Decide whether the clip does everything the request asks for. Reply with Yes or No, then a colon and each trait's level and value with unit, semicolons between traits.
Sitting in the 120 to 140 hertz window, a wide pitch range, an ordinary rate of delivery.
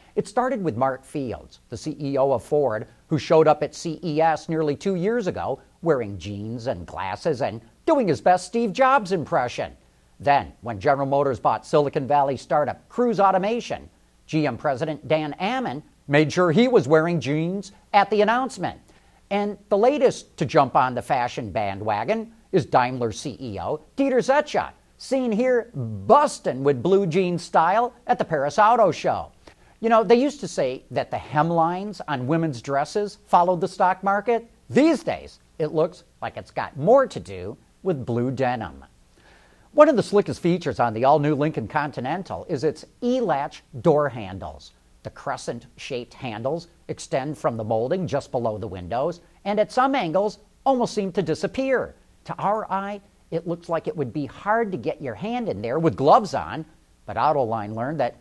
No: medium, 160 Hz; wide, 7.4 semitones; average, 170 wpm